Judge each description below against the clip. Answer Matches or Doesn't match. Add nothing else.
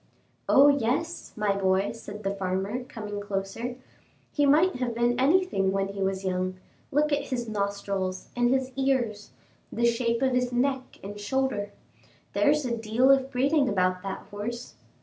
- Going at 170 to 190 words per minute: Doesn't match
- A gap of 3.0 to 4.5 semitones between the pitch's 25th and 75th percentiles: Doesn't match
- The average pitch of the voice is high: Matches